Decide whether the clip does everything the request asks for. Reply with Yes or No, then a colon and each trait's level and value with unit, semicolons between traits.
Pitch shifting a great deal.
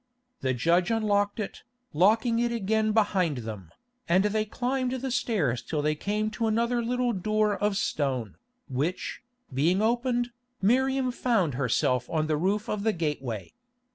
Yes: wide, 7.1 semitones